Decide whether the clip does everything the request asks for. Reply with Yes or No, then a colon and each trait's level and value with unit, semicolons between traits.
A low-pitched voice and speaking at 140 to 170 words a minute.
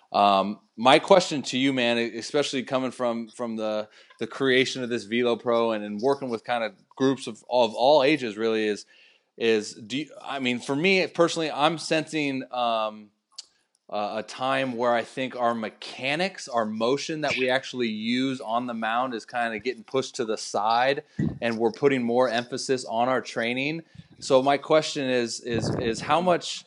No: low, 125 Hz; average, 185 wpm